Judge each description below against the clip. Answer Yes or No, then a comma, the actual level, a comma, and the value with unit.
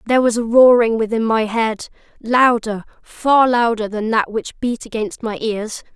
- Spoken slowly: No, average, 160 wpm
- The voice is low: No, high, 230 Hz